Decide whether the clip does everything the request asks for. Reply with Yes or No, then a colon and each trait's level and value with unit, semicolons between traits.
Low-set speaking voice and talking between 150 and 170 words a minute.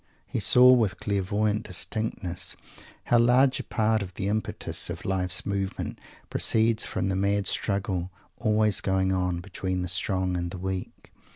Yes: low, 100 Hz; average, 155 wpm